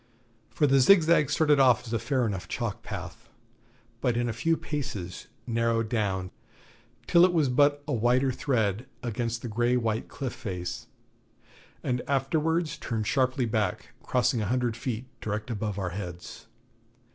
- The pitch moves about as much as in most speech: Yes, average, 3.8 semitones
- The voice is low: Yes, low, 120 Hz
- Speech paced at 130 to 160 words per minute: Yes, average, 155 wpm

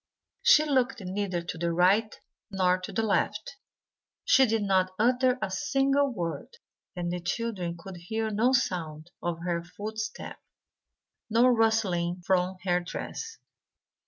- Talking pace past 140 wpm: No, slow, 135 wpm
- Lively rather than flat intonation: No, average, 4.7 semitones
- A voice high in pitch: Yes, high, 195 Hz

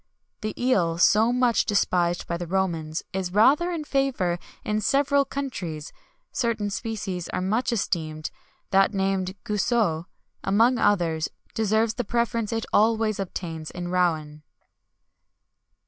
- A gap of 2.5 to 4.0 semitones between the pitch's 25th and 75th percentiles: No, average, 4.8 semitones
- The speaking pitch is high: Yes, high, 200 Hz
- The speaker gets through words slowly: Yes, slow, 125 wpm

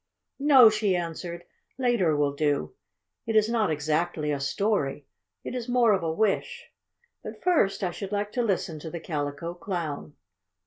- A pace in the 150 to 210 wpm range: Yes, average, 165 wpm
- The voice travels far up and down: Yes, wide, 5.9 semitones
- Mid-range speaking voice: Yes, medium, 175 Hz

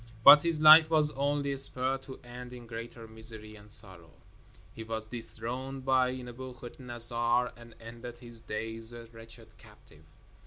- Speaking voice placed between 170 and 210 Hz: No, low, 120 Hz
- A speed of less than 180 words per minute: Yes, average, 145 wpm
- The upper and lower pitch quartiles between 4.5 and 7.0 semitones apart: No, narrow, 2.5 semitones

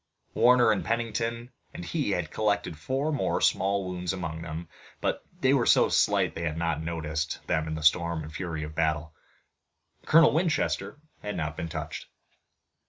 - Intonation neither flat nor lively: No, wide, 6.6 semitones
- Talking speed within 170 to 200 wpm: Yes, average, 175 wpm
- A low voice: Yes, very low, 85 Hz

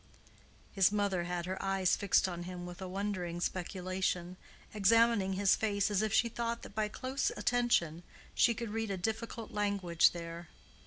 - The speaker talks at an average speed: Yes, average, 165 wpm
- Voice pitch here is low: No, high, 195 Hz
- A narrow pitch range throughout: No, average, 3.5 semitones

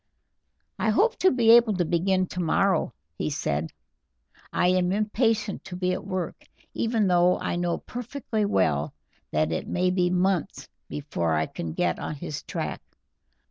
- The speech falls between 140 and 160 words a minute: Yes, average, 155 wpm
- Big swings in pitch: Yes, wide, 5.8 semitones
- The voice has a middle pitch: Yes, medium, 180 Hz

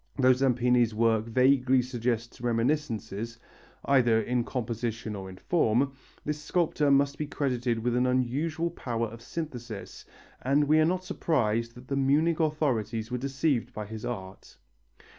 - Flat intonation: No, average, 3.5 semitones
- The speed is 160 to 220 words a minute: No, average, 145 wpm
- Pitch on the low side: Yes, low, 125 Hz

